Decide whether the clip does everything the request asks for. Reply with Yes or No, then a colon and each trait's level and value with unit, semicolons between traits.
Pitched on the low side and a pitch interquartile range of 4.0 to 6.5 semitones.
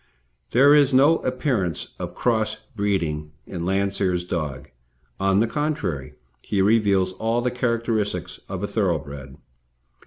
Yes: low, 100 Hz; average, 5.1 semitones